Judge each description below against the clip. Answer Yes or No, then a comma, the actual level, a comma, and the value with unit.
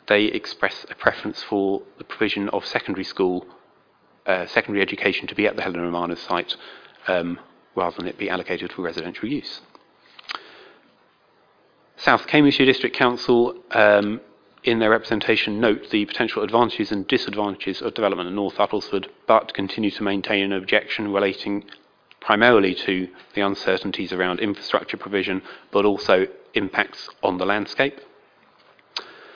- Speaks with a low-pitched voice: Yes, low, 100 Hz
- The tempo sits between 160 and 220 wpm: No, average, 140 wpm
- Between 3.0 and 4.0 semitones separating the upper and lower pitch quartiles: No, narrow, 2.4 semitones